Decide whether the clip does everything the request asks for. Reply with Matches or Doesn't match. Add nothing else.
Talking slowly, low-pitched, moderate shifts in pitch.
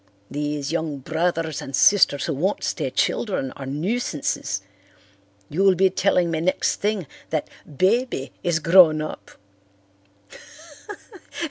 Doesn't match